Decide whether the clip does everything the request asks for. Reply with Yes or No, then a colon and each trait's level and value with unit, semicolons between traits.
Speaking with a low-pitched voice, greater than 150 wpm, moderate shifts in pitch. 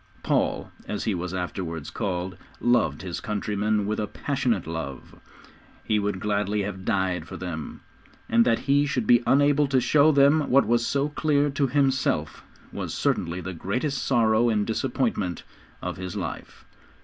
No: low, 105 Hz; average, 160 wpm; wide, 6.3 semitones